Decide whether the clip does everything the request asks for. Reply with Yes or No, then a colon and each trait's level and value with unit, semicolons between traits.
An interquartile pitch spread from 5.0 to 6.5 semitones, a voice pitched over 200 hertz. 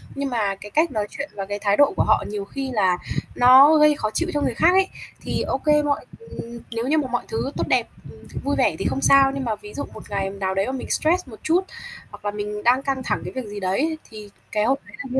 Yes: wide, 5.6 semitones; very high, 250 Hz